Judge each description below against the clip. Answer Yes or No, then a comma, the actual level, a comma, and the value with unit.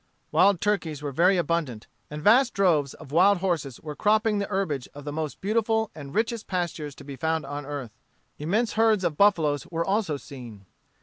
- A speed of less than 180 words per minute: No, average, 185 wpm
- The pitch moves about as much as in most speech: No, wide, 5.7 semitones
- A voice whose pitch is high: No, medium, 165 Hz